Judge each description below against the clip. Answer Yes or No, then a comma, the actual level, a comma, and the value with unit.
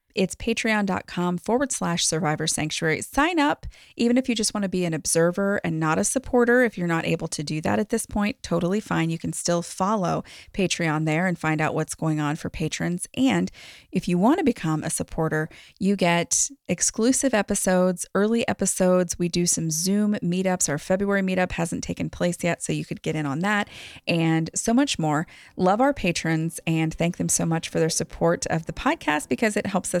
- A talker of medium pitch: Yes, medium, 175 Hz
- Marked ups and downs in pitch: No, average, 4.4 semitones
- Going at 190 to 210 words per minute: Yes, fast, 205 wpm